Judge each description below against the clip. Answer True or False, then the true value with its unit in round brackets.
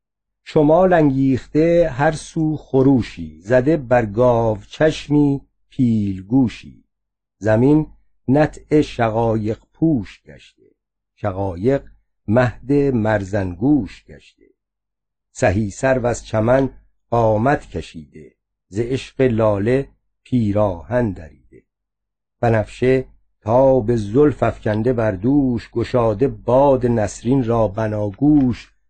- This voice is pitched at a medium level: False (120 Hz)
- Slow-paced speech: True (85 wpm)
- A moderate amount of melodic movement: True (4.2 semitones)